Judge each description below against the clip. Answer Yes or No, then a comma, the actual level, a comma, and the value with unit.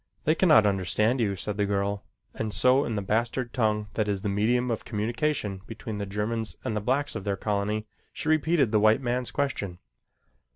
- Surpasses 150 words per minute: Yes, average, 195 wpm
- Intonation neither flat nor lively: Yes, average, 3.2 semitones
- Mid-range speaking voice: No, low, 110 Hz